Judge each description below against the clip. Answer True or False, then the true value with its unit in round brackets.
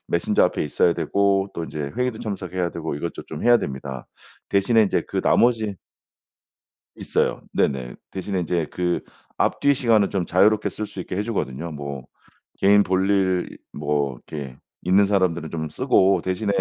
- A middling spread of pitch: True (4.3 semitones)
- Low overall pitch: True (95 Hz)